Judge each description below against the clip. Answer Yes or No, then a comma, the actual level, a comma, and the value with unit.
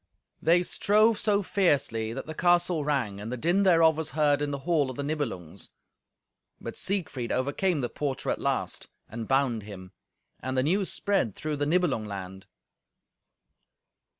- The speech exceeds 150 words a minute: Yes, average, 160 wpm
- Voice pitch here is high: No, medium, 145 Hz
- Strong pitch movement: Yes, wide, 6.7 semitones